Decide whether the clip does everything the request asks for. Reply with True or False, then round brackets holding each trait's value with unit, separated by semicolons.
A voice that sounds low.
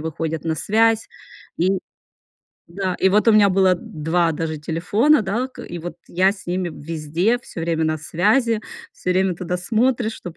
False (180 Hz)